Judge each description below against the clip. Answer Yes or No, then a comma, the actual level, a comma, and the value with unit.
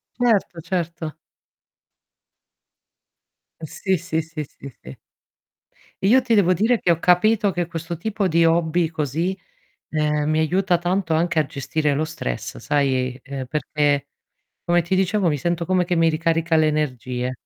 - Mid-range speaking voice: Yes, medium, 165 Hz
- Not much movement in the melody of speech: No, average, 3.0 semitones